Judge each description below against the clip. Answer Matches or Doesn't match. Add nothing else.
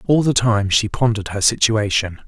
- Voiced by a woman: Doesn't match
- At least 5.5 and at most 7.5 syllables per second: Doesn't match